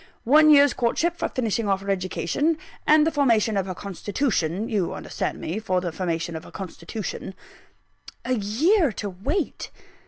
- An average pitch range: No, wide, 7.3 semitones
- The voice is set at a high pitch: Yes, high, 215 Hz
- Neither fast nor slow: Yes, average, 175 wpm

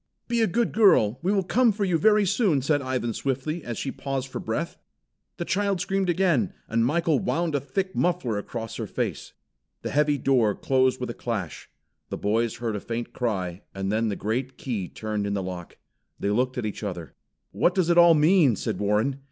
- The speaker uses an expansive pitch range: Yes, wide, 7.9 semitones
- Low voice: Yes, low, 130 Hz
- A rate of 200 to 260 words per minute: Yes, fast, 205 wpm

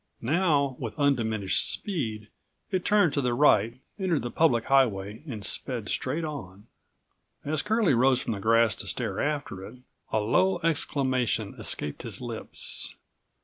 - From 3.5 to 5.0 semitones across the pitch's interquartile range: No, wide, 5.5 semitones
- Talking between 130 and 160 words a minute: Yes, average, 145 wpm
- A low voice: Yes, low, 130 Hz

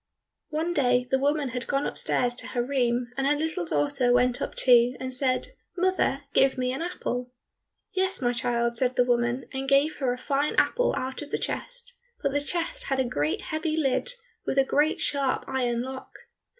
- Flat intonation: No, average, 3.3 semitones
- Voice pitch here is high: Yes, very high, 265 Hz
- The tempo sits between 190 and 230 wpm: Yes, average, 195 wpm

